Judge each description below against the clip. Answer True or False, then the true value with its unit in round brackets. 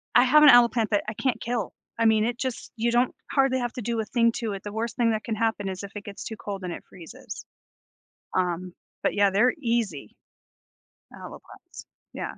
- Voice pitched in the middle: False (225 Hz)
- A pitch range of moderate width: True (3.0 semitones)